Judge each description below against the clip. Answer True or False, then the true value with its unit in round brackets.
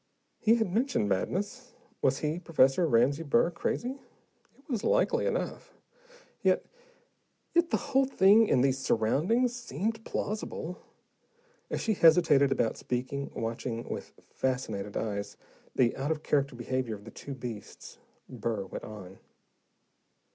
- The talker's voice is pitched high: False (140 Hz)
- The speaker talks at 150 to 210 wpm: False (135 wpm)